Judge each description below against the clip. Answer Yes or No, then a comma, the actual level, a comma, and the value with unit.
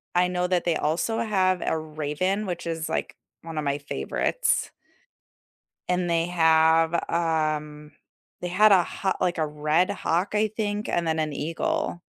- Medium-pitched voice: Yes, medium, 170 Hz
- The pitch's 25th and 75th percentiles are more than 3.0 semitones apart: No, average, 2.7 semitones